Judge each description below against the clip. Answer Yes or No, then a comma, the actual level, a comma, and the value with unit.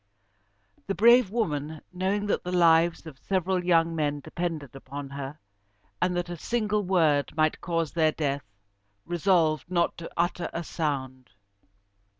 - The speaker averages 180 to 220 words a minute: No, average, 145 wpm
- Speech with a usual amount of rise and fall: Yes, average, 3.3 semitones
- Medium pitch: Yes, medium, 165 Hz